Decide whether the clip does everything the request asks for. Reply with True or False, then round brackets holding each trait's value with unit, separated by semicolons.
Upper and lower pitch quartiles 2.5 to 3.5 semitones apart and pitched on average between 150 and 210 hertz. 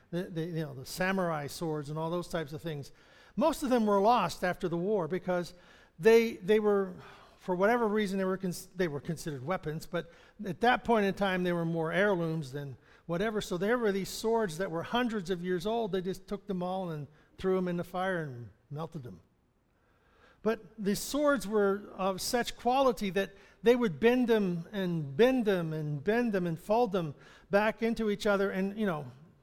False (4.1 semitones; 190 Hz)